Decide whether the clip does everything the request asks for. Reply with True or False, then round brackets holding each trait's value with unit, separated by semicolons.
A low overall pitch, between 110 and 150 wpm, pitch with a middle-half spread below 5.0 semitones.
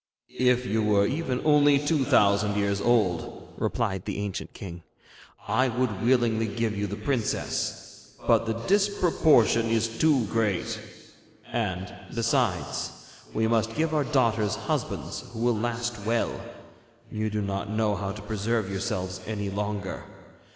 True (110 Hz; 140 wpm; 3.2 semitones)